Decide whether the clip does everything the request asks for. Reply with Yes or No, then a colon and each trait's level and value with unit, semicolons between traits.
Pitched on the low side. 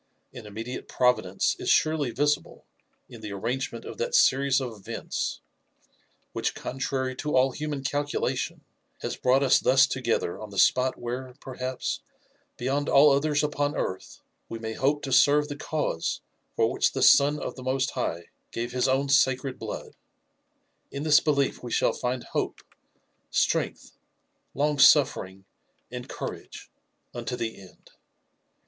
Yes: low, 130 Hz